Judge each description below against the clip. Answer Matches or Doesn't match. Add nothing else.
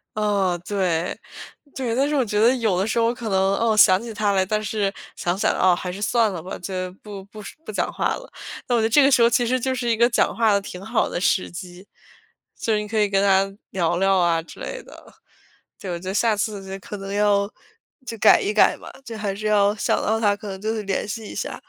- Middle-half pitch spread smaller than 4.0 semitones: Matches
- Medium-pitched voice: Doesn't match